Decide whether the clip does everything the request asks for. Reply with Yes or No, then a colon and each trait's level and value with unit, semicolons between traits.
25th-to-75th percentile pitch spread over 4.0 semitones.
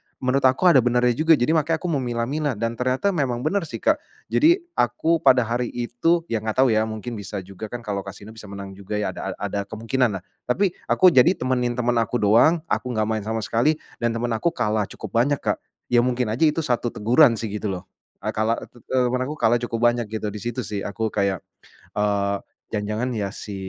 No: average, 3.3 semitones